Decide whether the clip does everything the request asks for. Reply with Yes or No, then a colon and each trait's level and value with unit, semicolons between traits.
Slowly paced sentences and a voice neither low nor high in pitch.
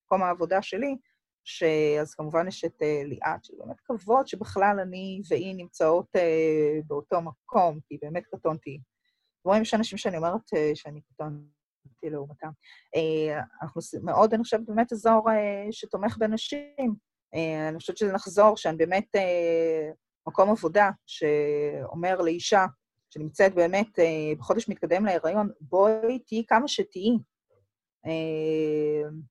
No: average, 135 wpm; medium, 170 Hz